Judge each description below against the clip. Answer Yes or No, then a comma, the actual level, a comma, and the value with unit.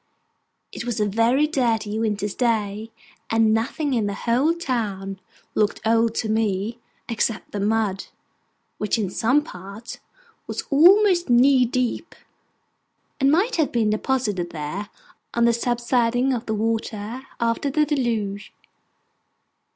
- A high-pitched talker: Yes, high, 230 Hz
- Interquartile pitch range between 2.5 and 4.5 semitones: Yes, average, 3.4 semitones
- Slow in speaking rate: Yes, slow, 130 wpm